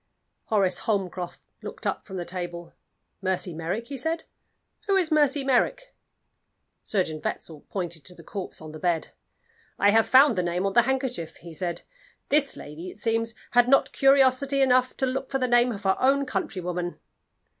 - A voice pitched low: No, high, 210 Hz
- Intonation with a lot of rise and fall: Yes, wide, 7.0 semitones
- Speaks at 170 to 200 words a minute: Yes, average, 175 wpm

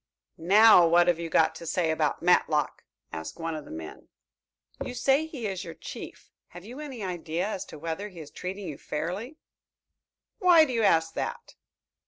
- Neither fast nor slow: Yes, average, 185 wpm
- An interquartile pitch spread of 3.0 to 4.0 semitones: No, average, 5.2 semitones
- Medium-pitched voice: Yes, medium, 175 Hz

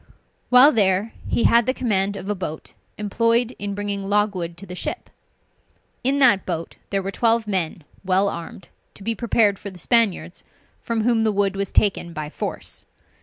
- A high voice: Yes, high, 200 Hz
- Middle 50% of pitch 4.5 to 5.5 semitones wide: No, average, 3.3 semitones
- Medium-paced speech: Yes, average, 175 wpm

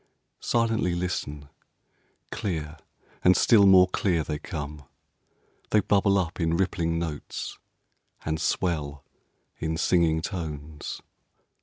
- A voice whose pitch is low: Yes, very low, 85 Hz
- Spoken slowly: Yes, slow, 105 wpm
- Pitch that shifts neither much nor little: Yes, average, 3.4 semitones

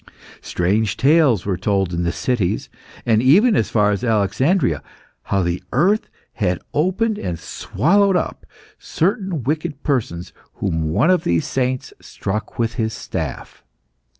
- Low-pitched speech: Yes, low, 115 Hz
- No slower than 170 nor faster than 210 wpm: No, average, 140 wpm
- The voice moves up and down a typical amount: No, wide, 8.8 semitones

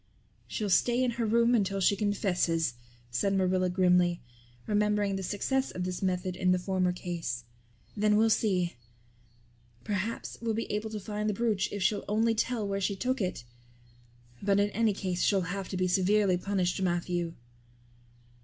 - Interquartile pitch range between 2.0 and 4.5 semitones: Yes, average, 2.7 semitones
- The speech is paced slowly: No, average, 165 wpm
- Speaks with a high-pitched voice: Yes, high, 195 Hz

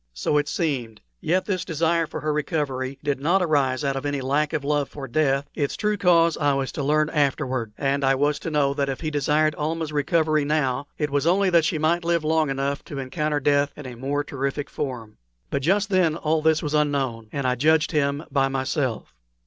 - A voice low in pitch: No, medium, 145 Hz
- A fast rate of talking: Yes, fast, 215 wpm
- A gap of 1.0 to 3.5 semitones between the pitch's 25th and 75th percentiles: Yes, narrow, 2.4 semitones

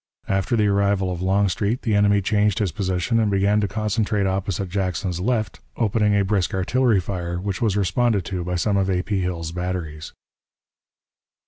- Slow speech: No, average, 170 wpm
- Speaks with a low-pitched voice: Yes, low, 100 Hz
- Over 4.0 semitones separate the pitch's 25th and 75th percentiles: No, narrow, 2.4 semitones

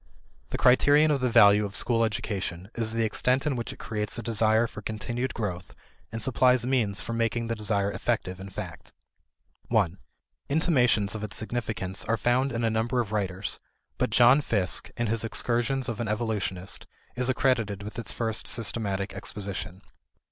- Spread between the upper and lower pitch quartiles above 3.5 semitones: No, average, 2.9 semitones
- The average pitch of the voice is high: No, low, 115 Hz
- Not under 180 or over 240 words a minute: No, average, 170 wpm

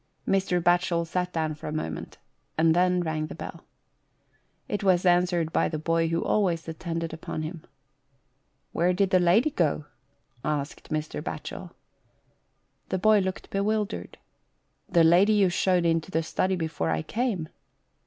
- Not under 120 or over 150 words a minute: No, average, 160 wpm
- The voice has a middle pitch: Yes, medium, 170 Hz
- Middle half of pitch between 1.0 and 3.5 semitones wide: Yes, average, 2.8 semitones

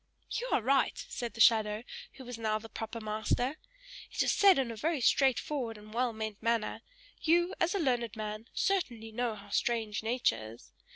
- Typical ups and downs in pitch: Yes, average, 3.4 semitones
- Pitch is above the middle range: Yes, high, 230 Hz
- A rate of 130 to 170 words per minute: No, average, 190 wpm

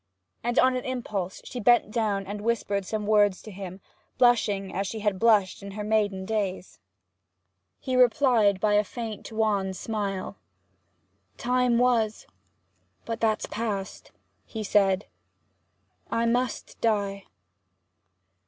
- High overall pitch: Yes, high, 215 Hz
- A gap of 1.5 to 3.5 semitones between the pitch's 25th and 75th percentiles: Yes, average, 2.7 semitones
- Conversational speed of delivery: No, slow, 125 wpm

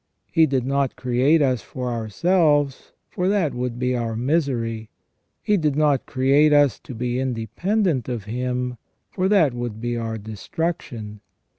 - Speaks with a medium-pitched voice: No, low, 130 Hz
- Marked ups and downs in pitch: No, average, 4.2 semitones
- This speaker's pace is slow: No, average, 150 wpm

